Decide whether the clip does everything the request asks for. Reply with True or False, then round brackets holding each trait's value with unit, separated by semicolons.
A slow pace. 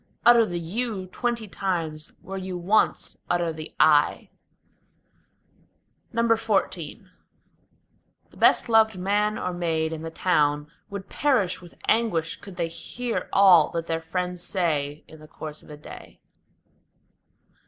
True (130 wpm)